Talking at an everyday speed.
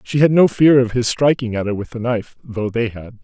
No: fast, 280 wpm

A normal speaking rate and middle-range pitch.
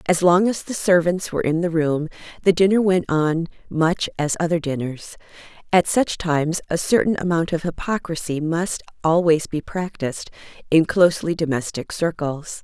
Yes: average, 155 wpm; medium, 165 Hz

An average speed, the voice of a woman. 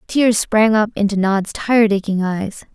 Yes: average, 175 wpm; female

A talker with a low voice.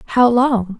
No: high, 235 Hz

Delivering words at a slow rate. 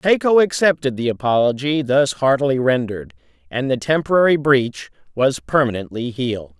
Yes: slow, 125 wpm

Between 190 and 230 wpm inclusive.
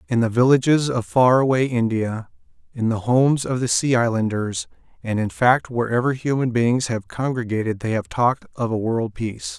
No: average, 180 wpm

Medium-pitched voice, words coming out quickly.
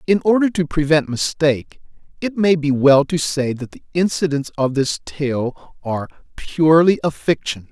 No: medium, 150 Hz; average, 165 wpm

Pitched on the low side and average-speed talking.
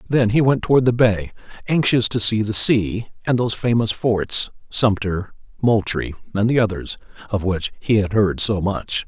Yes: low, 110 Hz; average, 180 wpm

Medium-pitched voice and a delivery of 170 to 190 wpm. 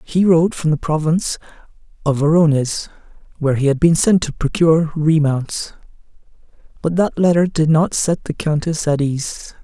No: medium, 155 Hz; average, 155 wpm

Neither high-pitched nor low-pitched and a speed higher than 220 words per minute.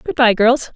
No: high, 245 Hz; fast, 240 wpm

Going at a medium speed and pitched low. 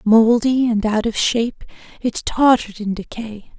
No: average, 150 wpm; high, 225 Hz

